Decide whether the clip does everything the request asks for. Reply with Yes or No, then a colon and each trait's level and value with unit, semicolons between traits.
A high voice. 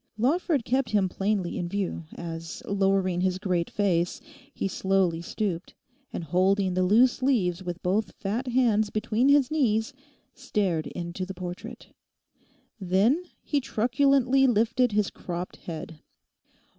Yes: high, 200 Hz